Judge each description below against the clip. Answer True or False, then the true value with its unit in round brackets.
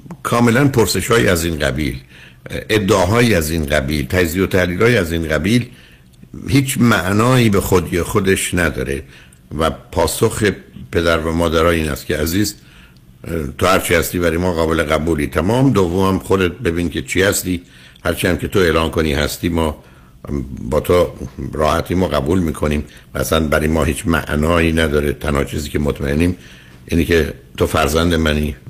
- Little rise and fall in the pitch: False (4.4 semitones)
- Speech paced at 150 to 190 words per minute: True (155 wpm)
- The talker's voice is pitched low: True (80 Hz)